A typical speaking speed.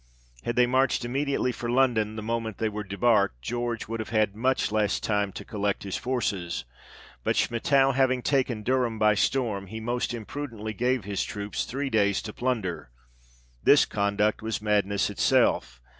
Yes: average, 165 wpm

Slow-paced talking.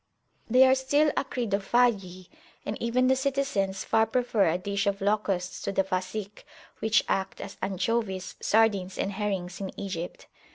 No: average, 150 wpm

